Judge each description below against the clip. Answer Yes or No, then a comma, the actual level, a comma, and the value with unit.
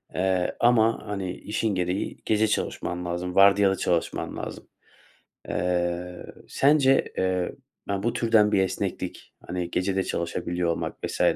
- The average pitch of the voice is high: No, very low, 95 Hz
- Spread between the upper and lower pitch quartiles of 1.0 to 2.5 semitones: No, average, 2.9 semitones